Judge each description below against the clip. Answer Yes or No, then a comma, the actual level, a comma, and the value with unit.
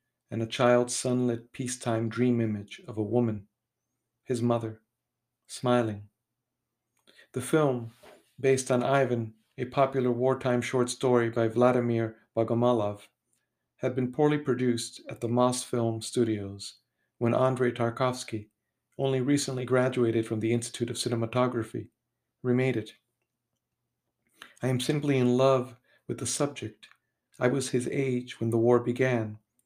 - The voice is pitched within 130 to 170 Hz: No, low, 120 Hz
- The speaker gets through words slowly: Yes, slow, 130 wpm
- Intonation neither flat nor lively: No, narrow, 1.8 semitones